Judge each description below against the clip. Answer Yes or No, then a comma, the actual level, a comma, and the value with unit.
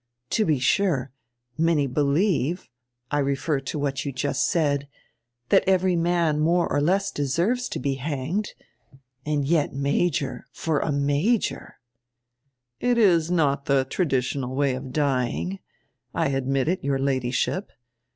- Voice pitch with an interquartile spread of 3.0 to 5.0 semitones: Yes, average, 4.2 semitones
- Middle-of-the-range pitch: Yes, medium, 145 Hz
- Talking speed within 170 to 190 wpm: No, average, 150 wpm